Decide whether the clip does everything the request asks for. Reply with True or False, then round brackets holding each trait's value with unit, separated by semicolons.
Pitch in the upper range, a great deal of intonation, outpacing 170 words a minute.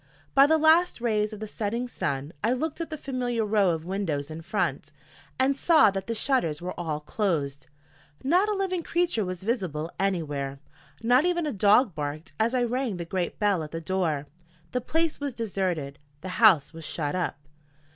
True (205 Hz; 7.7 semitones; 185 wpm)